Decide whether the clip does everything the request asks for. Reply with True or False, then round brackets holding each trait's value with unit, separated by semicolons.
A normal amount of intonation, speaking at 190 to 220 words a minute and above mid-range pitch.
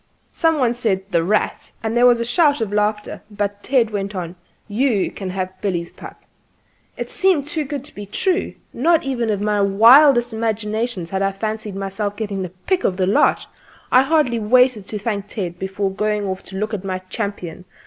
True (3.8 semitones; 195 wpm; 210 Hz)